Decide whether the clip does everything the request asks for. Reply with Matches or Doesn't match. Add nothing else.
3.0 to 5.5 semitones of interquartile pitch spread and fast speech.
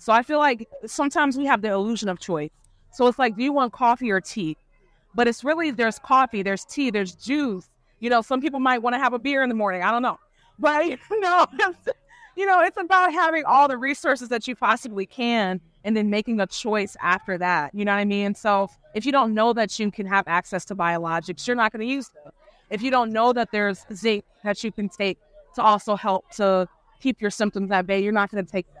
Matches